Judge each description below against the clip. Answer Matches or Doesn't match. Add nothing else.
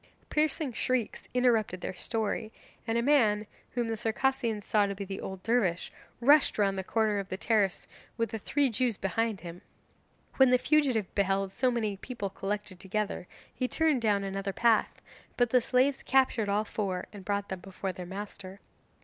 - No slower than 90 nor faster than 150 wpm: Doesn't match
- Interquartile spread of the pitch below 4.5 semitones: Matches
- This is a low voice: Doesn't match